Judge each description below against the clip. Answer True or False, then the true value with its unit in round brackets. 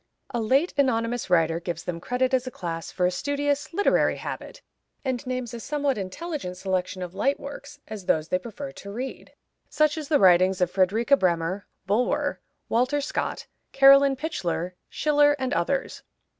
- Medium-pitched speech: False (240 Hz)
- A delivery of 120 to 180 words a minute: True (165 wpm)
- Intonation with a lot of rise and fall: True (7.4 semitones)